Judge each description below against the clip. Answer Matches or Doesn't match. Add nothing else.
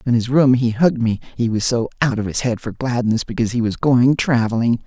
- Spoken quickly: Matches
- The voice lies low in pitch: Matches